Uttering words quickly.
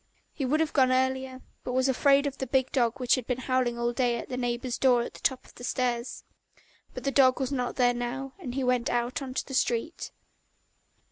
Yes: fast, 225 wpm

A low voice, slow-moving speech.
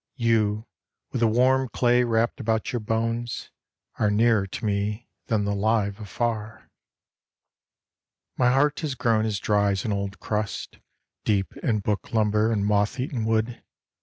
No: low, 110 Hz; average, 150 wpm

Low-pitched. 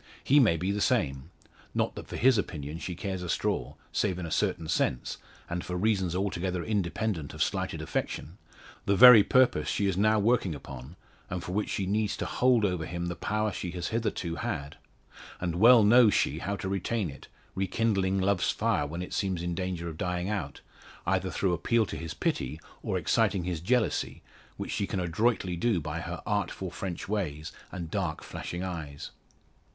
Yes: very low, 90 Hz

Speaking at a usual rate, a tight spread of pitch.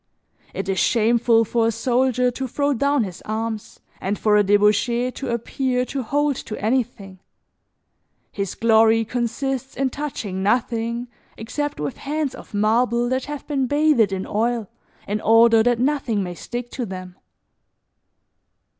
No: average, 145 wpm; average, 3.4 semitones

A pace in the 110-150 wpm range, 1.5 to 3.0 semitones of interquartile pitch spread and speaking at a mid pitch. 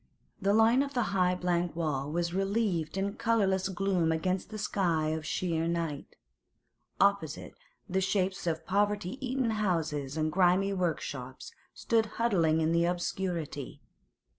No: average, 140 wpm; average, 3.6 semitones; medium, 180 Hz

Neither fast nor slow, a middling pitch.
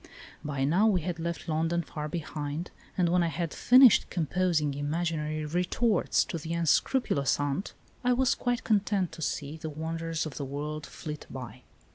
Yes: average, 165 wpm; medium, 165 Hz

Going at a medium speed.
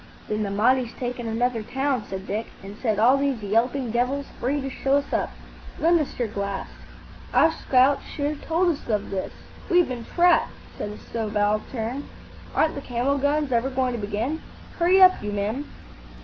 Yes: average, 180 wpm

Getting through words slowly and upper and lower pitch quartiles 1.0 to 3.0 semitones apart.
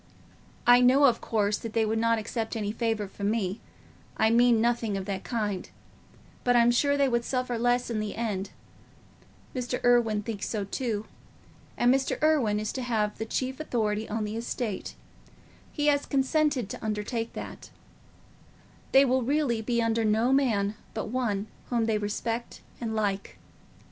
No: average, 155 wpm; narrow, 2.6 semitones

